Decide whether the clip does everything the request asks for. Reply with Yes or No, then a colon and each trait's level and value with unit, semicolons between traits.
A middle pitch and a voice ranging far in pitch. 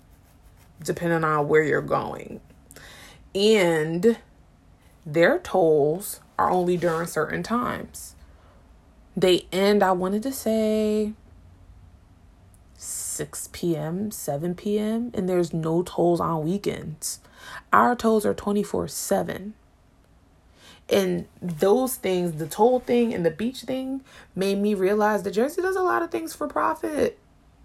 Yes: medium, 175 Hz; wide, 7.0 semitones